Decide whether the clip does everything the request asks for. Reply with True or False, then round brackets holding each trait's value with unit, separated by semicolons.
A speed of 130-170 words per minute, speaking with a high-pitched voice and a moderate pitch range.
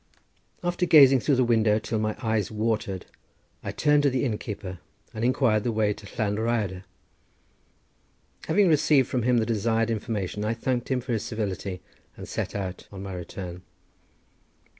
False (160 wpm; 110 Hz; 3.5 semitones)